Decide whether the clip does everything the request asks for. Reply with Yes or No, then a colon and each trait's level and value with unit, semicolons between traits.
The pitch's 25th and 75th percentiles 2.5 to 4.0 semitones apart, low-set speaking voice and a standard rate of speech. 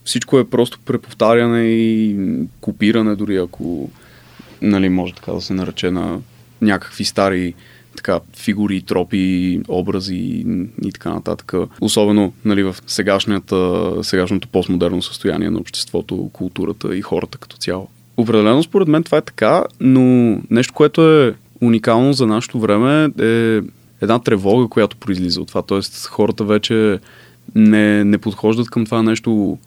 Yes: average, 3.3 semitones; low, 105 Hz; average, 135 wpm